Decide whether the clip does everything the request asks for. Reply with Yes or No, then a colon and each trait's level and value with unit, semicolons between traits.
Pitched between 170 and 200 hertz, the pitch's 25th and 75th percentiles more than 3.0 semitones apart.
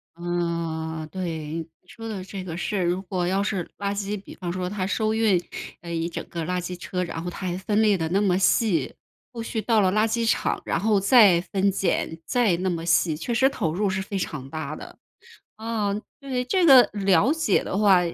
Yes: high, 190 Hz; average, 3.5 semitones